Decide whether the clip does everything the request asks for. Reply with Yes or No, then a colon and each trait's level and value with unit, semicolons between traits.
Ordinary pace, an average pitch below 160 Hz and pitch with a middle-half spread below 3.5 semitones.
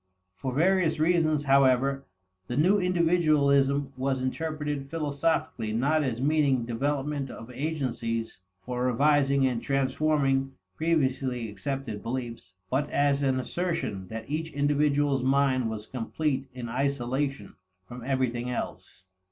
No: slow, 120 wpm; low, 135 Hz; average, 2.9 semitones